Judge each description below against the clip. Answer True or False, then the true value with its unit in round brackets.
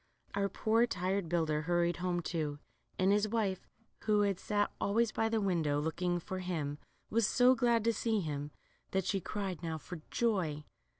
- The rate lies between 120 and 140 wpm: False (175 wpm)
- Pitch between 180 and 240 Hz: True (185 Hz)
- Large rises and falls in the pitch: False (4.2 semitones)